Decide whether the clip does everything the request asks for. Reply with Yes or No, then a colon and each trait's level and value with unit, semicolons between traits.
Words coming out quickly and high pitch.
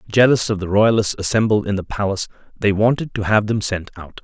No: fast, 210 wpm; low, 105 Hz